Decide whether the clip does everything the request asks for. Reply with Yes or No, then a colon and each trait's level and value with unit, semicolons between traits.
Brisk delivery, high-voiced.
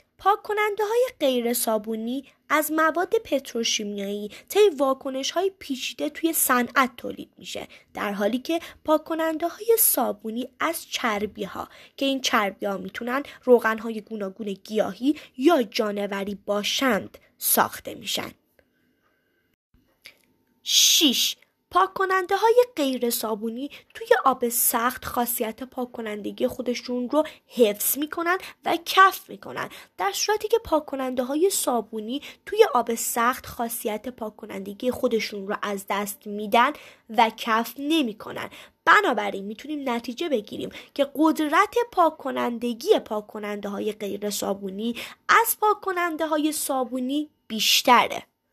No: average, 110 wpm; very high, 255 Hz